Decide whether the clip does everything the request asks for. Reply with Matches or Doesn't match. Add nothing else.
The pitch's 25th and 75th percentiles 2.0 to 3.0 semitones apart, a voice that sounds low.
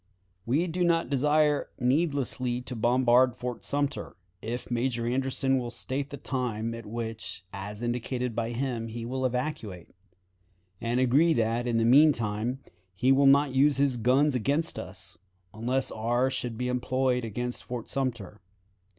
Matches